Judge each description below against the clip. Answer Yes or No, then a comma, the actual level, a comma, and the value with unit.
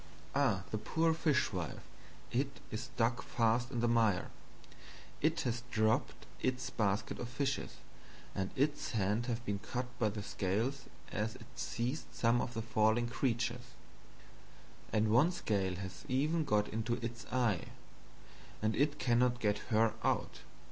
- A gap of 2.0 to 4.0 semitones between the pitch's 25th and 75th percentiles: Yes, average, 2.9 semitones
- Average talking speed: Yes, average, 145 wpm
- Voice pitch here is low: Yes, low, 120 Hz